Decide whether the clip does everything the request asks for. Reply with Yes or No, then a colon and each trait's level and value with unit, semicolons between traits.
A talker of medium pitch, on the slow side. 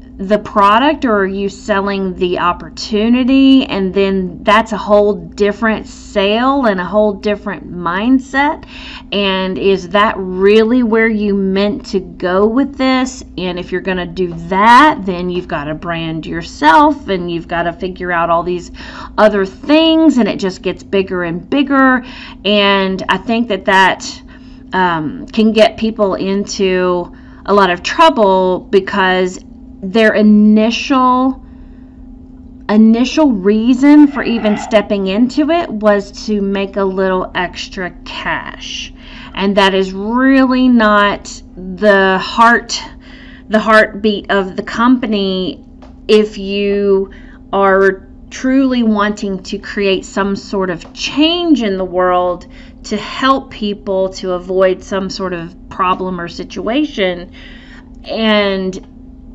No: high, 205 Hz; slow, 130 wpm